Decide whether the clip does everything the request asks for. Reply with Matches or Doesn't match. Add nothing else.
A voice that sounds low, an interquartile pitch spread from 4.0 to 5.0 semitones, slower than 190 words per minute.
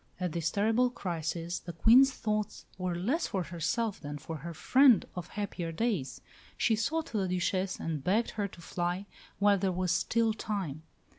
Doesn't match